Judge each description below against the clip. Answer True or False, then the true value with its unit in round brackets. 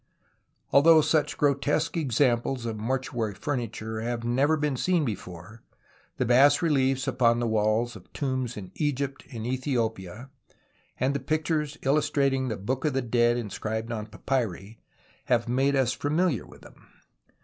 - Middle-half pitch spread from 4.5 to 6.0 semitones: False (3.8 semitones)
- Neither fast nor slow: True (150 wpm)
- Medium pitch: False (130 Hz)